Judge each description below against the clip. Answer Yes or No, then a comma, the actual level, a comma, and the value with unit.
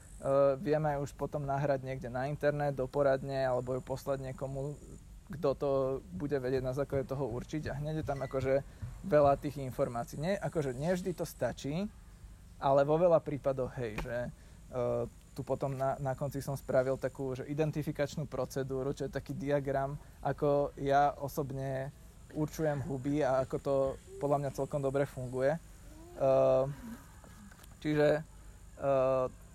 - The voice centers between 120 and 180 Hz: Yes, low, 135 Hz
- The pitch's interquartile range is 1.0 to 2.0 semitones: Yes, narrow, 1.7 semitones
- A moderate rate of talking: Yes, average, 150 wpm